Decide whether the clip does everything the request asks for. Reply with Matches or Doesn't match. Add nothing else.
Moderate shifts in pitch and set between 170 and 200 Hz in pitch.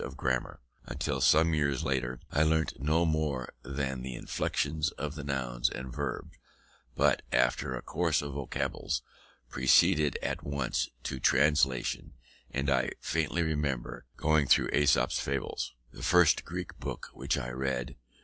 Doesn't match